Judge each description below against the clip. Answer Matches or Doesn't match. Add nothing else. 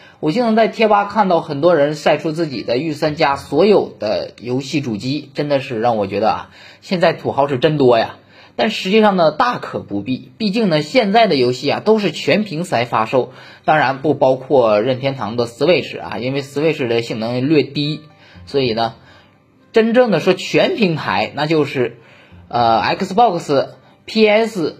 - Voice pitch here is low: Doesn't match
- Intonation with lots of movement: Matches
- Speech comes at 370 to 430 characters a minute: Doesn't match